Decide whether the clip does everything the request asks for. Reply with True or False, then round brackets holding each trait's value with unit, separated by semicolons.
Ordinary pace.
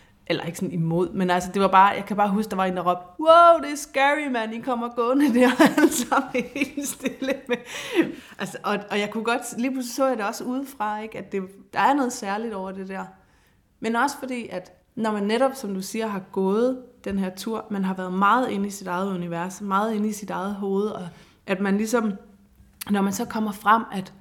False (235 wpm)